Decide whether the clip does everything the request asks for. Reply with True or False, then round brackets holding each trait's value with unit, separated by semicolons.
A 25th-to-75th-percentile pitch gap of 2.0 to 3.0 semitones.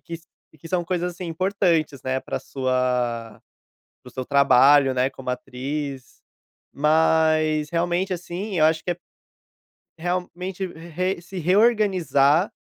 False (4.5 semitones)